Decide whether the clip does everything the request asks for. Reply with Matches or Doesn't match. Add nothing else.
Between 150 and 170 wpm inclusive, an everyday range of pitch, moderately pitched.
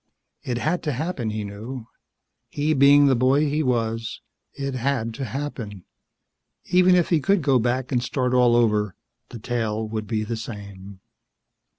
Doesn't match